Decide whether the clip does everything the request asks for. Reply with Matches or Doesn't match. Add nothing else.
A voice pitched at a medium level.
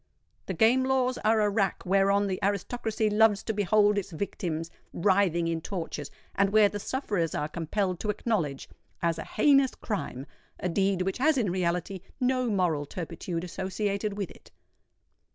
Doesn't match